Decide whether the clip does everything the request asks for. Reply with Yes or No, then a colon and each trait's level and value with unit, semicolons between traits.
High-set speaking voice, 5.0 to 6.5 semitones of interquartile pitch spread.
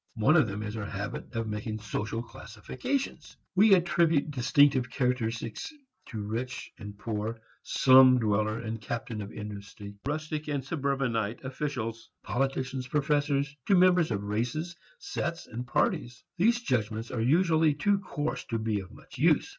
No: low, 125 Hz; average, 5.3 semitones